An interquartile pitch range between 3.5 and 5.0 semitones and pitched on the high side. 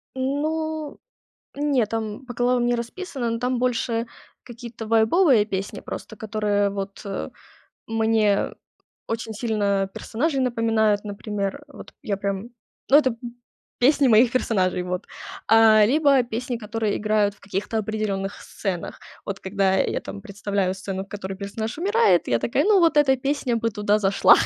Yes: average, 3.8 semitones; high, 225 Hz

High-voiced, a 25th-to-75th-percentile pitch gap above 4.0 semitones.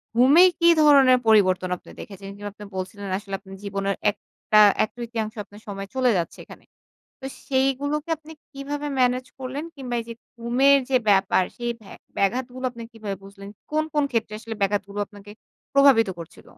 Yes: high, 230 Hz; average, 4.9 semitones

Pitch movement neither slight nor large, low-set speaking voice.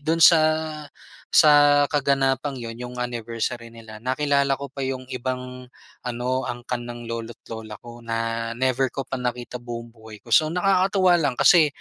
Yes: average, 3.1 semitones; low, 125 Hz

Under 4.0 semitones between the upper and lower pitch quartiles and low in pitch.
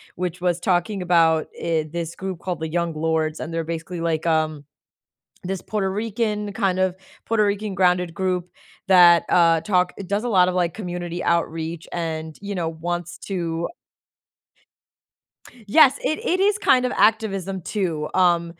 No: average, 2.8 semitones; medium, 175 Hz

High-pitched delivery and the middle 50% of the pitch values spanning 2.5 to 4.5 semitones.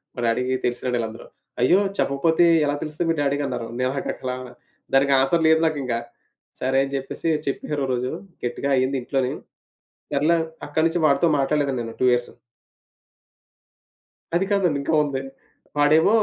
No: medium, 140 Hz; average, 3.2 semitones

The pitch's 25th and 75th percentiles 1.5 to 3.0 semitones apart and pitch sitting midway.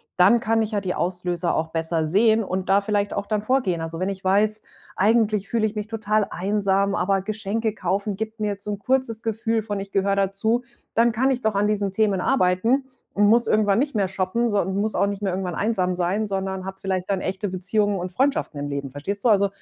No: narrow, 2.5 semitones; high, 200 Hz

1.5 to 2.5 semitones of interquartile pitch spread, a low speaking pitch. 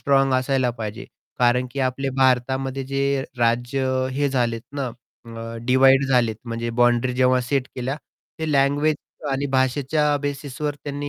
Yes: narrow, 2.2 semitones; low, 130 Hz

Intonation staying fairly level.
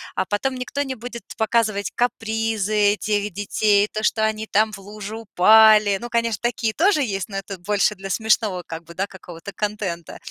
Yes: narrow, 2.1 semitones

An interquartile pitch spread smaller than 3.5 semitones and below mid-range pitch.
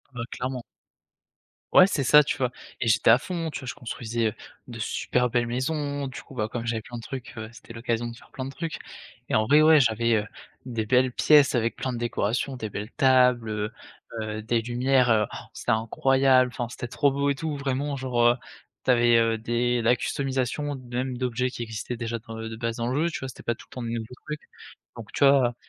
Yes: narrow, 2.5 semitones; low, 125 Hz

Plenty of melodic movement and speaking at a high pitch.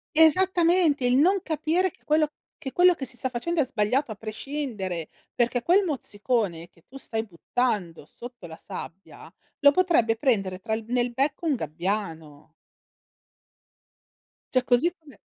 Yes: wide, 6.8 semitones; high, 245 Hz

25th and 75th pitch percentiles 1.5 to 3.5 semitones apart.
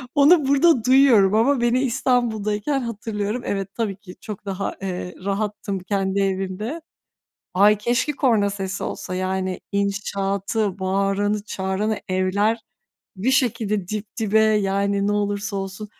Yes: narrow, 2.6 semitones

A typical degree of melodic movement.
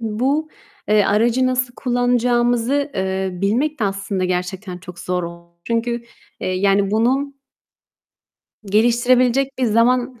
Yes: average, 4.4 semitones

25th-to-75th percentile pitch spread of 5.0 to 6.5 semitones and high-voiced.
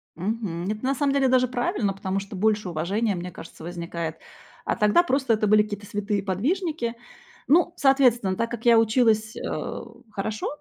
No: average, 4.1 semitones; high, 215 Hz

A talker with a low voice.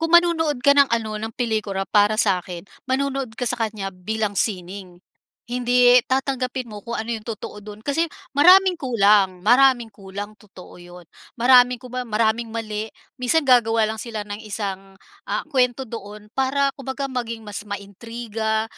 No: high, 225 Hz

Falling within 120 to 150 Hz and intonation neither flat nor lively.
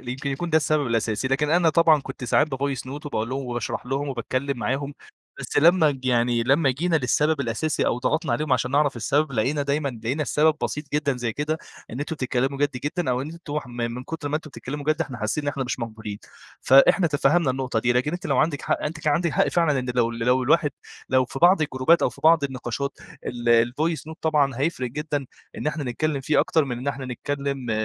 Yes: medium, 140 Hz; average, 3.3 semitones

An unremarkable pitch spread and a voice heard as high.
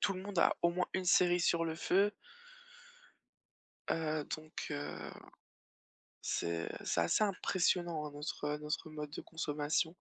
No: average, 3.2 semitones; medium, 160 Hz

